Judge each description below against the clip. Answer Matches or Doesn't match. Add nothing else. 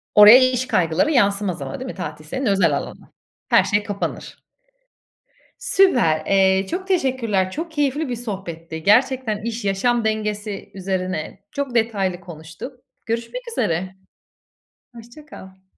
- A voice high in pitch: Matches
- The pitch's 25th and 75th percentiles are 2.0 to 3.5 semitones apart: Doesn't match